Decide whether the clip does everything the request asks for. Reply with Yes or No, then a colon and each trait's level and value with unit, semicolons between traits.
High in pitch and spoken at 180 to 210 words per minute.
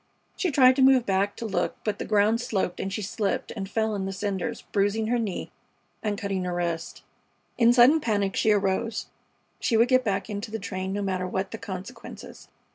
Yes: high, 205 Hz; average, 200 wpm